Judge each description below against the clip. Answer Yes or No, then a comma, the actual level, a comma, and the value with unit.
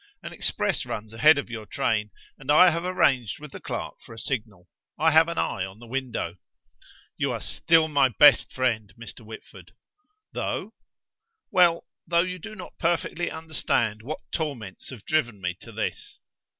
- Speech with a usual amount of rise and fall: No, wide, 6.5 semitones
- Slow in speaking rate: No, average, 170 wpm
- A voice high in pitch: No, low, 130 Hz